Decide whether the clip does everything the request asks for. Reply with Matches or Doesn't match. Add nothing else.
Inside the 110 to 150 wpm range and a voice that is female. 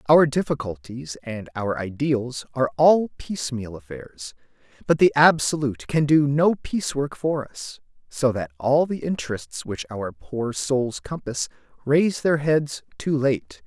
Doesn't match